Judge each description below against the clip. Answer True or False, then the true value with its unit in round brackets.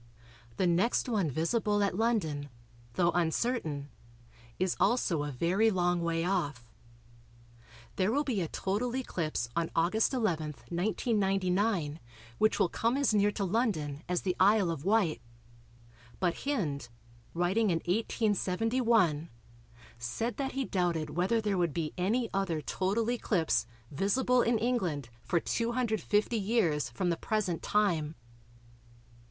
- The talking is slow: True (130 wpm)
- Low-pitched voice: False (190 Hz)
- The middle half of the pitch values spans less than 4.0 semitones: False (5.3 semitones)